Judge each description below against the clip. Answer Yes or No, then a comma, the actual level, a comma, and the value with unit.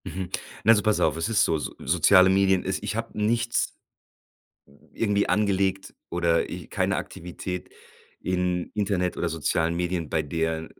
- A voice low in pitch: Yes, very low, 90 Hz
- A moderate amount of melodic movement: Yes, average, 3.2 semitones